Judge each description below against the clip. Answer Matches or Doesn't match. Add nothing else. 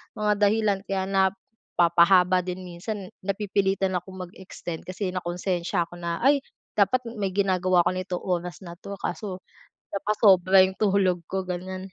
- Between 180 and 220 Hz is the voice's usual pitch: Matches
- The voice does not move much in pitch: Matches